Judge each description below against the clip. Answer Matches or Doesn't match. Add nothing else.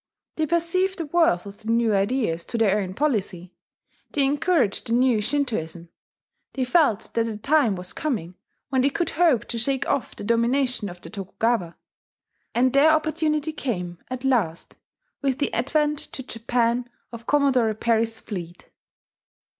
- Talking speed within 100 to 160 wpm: Matches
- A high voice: Matches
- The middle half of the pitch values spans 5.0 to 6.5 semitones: Matches